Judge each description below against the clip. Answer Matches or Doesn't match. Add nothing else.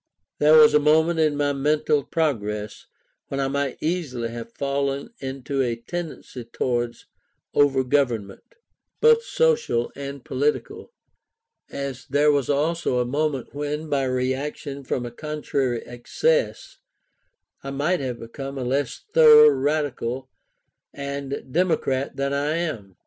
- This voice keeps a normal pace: Doesn't match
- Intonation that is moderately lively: Matches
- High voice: Doesn't match